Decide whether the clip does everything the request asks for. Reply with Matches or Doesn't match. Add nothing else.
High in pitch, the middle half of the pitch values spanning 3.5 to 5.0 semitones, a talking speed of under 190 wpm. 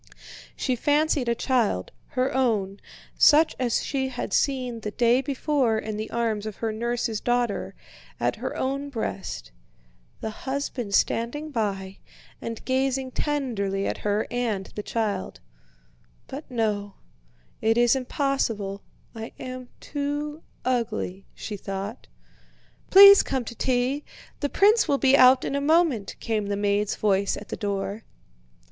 Matches